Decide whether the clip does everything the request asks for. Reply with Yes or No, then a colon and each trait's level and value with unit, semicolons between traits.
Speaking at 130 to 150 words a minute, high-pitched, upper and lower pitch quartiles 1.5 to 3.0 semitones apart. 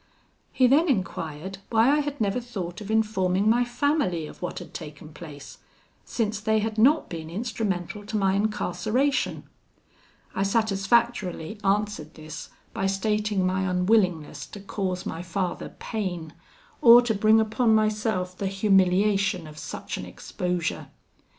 No: average, 140 wpm; high, 200 Hz; average, 3.5 semitones